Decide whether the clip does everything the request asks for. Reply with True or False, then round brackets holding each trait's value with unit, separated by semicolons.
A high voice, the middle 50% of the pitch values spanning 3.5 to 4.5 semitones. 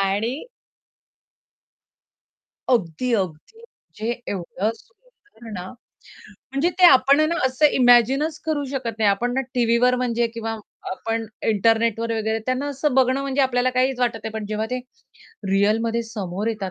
False (235 Hz; 3.1 semitones)